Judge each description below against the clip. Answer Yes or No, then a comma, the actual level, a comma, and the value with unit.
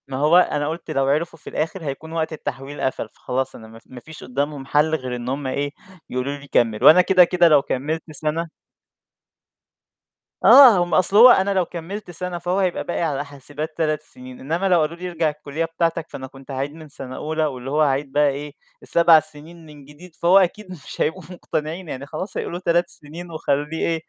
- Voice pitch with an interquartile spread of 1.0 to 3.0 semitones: No, average, 3.4 semitones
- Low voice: No, medium, 155 Hz